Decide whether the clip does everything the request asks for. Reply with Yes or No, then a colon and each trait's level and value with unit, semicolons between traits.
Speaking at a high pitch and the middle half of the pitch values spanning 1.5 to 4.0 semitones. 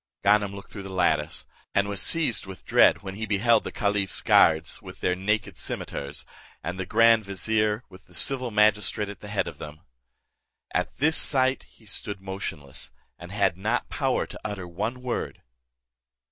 No: low, 100 Hz; average, 2.8 semitones